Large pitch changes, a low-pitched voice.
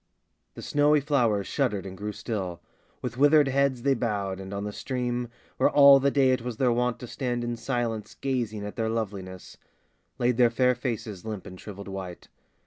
No: average, 4.0 semitones; low, 120 Hz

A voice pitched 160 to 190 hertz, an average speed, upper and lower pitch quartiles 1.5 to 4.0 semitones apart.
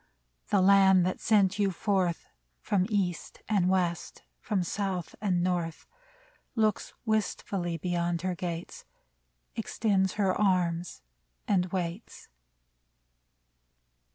No: medium, 185 Hz; slow, 100 wpm; narrow, 2.4 semitones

